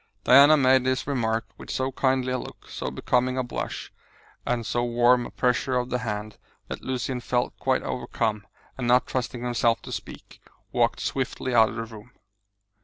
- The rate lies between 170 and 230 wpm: Yes, average, 180 wpm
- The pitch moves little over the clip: Yes, narrow, 1.8 semitones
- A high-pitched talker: No, low, 125 Hz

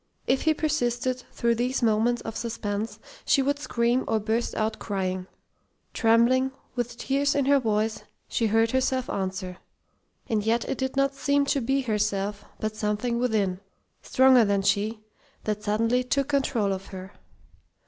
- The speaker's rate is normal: Yes, average, 155 wpm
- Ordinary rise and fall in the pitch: Yes, average, 3.7 semitones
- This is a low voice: No, high, 230 Hz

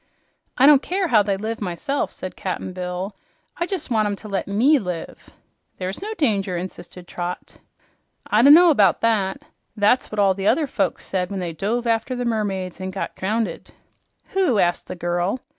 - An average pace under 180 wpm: No, average, 185 wpm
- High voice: Yes, high, 205 Hz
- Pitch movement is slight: No, average, 4.6 semitones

